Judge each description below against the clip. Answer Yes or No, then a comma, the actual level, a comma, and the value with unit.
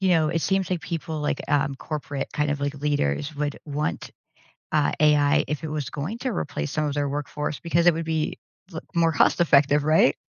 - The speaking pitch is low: No, medium, 150 Hz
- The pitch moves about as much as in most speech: No, narrow, 2.1 semitones